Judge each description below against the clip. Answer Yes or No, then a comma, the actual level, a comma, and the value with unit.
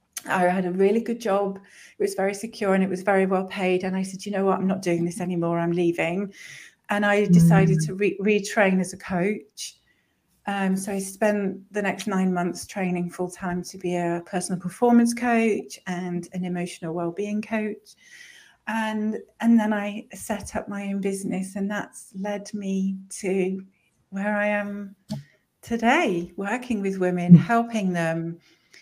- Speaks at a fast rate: No, average, 175 wpm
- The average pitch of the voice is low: No, high, 195 Hz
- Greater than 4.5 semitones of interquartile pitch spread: No, narrow, 2.4 semitones